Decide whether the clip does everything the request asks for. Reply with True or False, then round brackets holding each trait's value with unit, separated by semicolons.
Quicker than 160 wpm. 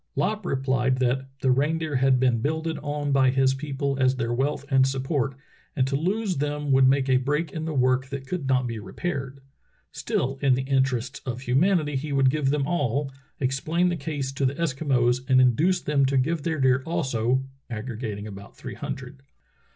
True (190 wpm)